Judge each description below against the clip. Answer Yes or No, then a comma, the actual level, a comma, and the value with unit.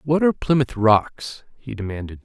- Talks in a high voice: No, low, 125 Hz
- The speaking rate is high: No, average, 160 wpm